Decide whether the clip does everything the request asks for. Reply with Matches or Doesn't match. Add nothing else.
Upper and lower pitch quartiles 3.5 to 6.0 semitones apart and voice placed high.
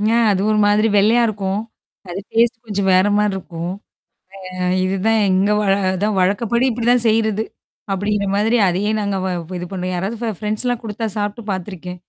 Doesn't match